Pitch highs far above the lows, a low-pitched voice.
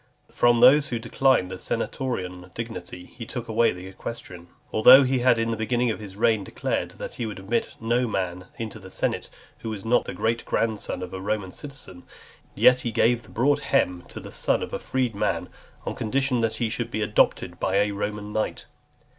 No: average, 3.7 semitones; low, 115 Hz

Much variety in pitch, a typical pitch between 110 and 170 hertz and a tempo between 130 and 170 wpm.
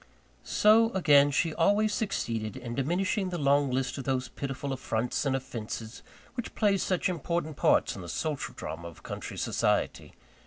Yes: wide, 6.2 semitones; medium, 140 Hz; average, 160 wpm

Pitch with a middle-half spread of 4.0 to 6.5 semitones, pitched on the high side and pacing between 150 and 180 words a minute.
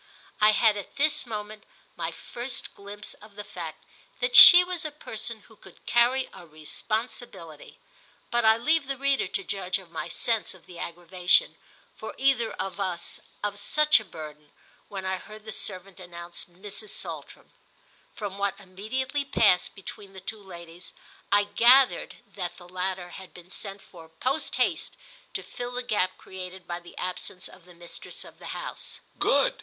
Yes: average, 4.4 semitones; high, 200 Hz; average, 170 wpm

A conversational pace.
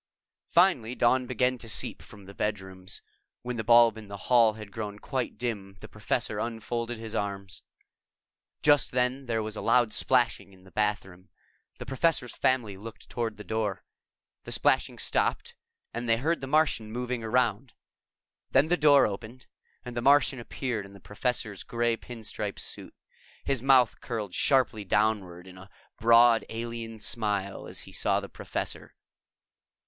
Yes: average, 160 wpm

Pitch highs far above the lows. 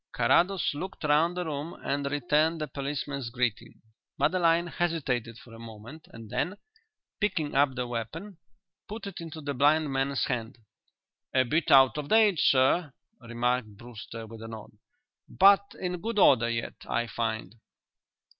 Yes: wide, 5.9 semitones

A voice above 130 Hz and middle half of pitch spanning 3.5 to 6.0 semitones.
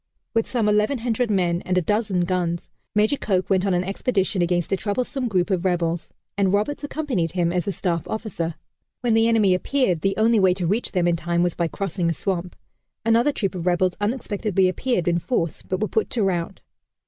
Yes: high, 190 Hz; average, 3.8 semitones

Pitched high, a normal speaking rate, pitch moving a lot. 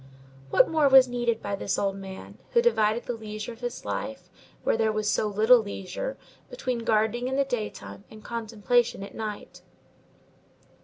No: high, 225 Hz; average, 165 wpm; average, 2.7 semitones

